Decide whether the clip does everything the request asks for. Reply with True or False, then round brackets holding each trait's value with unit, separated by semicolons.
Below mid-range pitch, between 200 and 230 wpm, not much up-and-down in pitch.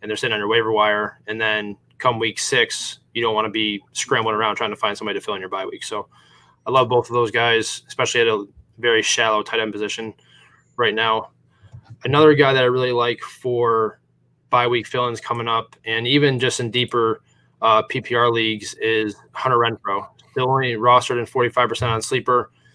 True (115 Hz; 205 wpm; 2.1 semitones)